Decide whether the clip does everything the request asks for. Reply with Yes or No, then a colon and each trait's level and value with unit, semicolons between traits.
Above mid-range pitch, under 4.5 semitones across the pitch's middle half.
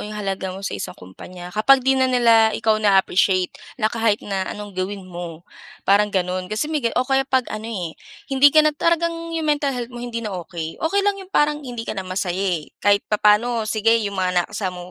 No: high, 215 Hz; average, 5.3 semitones